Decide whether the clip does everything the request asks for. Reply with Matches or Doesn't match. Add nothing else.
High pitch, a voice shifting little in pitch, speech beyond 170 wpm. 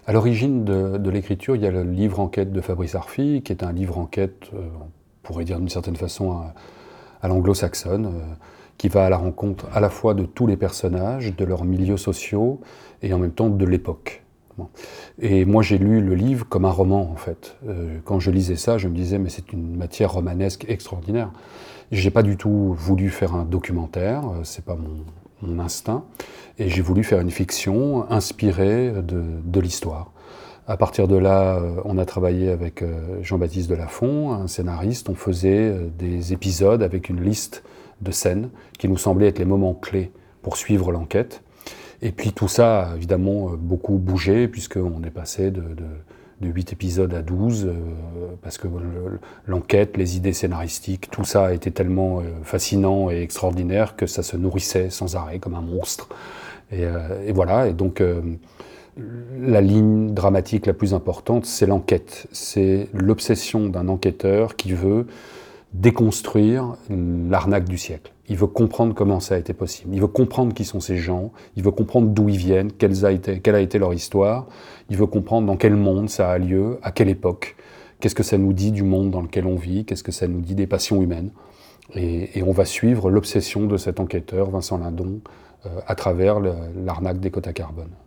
Doesn't match